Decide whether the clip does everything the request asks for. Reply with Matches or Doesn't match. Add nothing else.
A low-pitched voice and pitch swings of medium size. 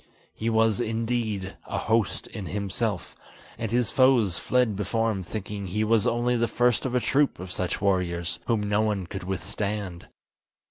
Matches